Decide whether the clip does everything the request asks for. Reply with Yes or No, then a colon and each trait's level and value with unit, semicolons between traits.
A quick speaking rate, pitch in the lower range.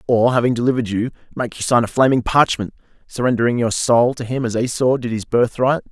Yes: fast, 215 wpm; low, 120 Hz